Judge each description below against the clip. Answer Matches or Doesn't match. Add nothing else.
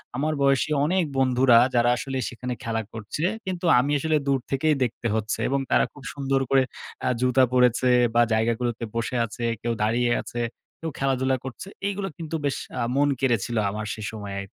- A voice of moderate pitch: Doesn't match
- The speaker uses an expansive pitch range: Doesn't match